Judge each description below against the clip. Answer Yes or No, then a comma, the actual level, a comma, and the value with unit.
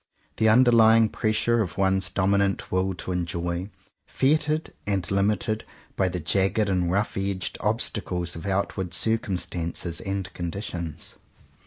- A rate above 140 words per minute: No, slow, 135 wpm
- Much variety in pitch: No, average, 3.2 semitones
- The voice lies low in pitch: Yes, very low, 95 Hz